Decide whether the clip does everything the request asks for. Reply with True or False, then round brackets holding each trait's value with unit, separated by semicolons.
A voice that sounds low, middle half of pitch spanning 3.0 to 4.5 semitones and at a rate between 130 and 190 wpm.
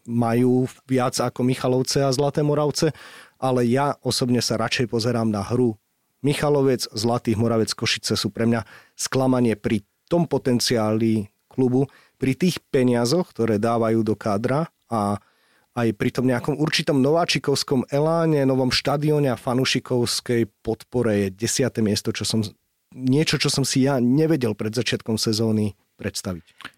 True (125 Hz; 3.4 semitones; 140 wpm)